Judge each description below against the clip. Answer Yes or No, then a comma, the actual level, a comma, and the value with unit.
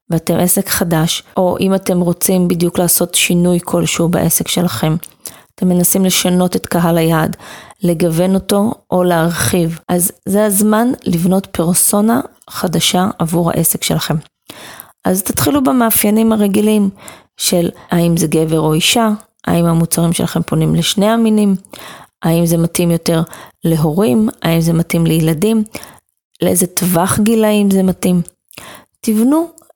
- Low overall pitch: No, medium, 180 Hz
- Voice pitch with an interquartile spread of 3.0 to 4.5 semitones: Yes, average, 3.7 semitones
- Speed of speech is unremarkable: Yes, average, 125 wpm